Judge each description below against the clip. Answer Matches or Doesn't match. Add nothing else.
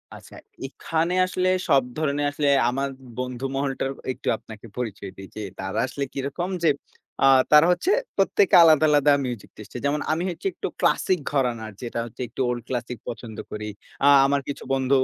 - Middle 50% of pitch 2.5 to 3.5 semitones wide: Doesn't match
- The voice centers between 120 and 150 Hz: Matches